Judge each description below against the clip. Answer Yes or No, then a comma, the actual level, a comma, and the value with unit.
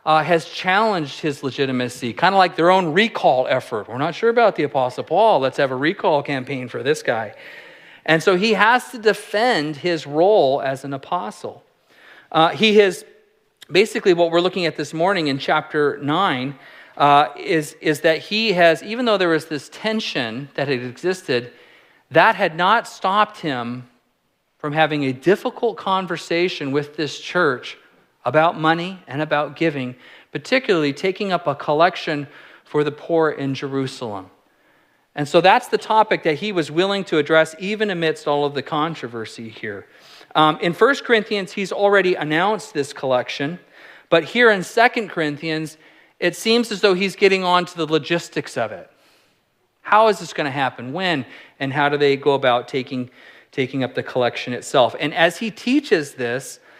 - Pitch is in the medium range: Yes, medium, 160 Hz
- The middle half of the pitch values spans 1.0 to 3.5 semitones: No, wide, 5.5 semitones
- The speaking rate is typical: Yes, average, 170 wpm